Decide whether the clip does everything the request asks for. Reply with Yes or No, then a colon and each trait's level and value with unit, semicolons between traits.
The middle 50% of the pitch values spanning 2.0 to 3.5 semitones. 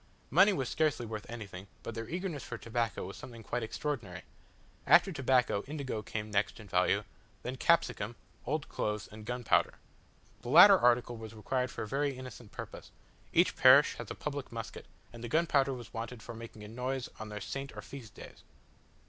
No: average, 4.0 semitones